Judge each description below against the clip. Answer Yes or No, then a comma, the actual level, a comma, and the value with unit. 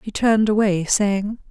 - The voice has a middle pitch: No, high, 205 Hz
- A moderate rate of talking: Yes, average, 160 wpm